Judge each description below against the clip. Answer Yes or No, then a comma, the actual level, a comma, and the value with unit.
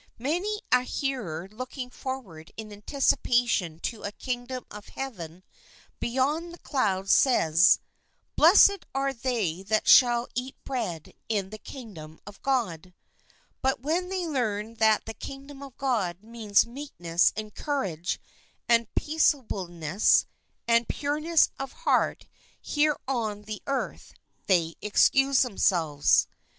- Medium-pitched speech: No, high, 235 Hz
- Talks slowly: Yes, slow, 125 wpm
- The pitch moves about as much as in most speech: No, wide, 5.7 semitones